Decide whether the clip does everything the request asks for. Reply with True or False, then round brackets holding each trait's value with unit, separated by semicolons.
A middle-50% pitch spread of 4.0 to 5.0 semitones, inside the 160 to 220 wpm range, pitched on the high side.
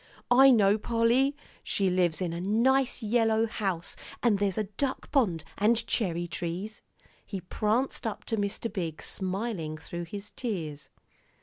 False (4.4 semitones; 145 wpm; 205 Hz)